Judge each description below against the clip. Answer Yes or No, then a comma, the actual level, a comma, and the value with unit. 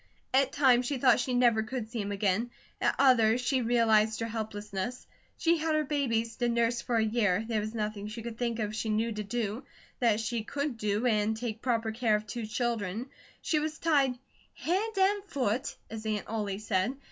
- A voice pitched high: Yes, high, 230 Hz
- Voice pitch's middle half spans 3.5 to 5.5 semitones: No, average, 2.9 semitones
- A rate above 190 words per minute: Yes, average, 200 wpm